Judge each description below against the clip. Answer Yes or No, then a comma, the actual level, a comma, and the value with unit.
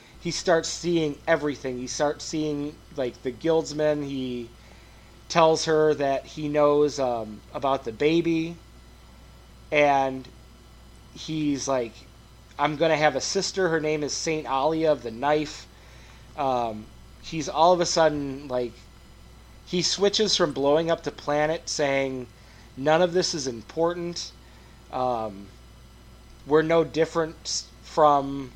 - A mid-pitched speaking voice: Yes, medium, 145 Hz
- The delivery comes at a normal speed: No, slow, 130 wpm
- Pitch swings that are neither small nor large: Yes, average, 5.0 semitones